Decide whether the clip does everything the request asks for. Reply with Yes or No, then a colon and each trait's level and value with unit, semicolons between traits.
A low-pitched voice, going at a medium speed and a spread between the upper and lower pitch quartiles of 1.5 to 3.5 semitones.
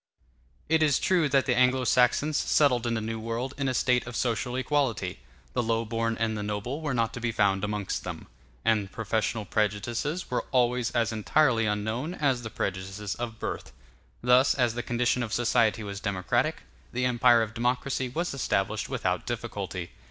Yes: low, 120 Hz; average, 180 wpm; narrow, 2.6 semitones